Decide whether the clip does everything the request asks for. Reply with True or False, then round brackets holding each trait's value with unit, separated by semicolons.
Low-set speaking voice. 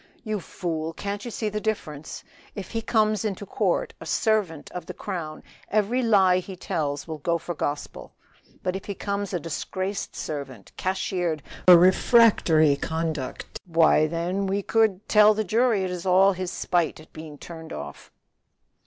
False (185 Hz)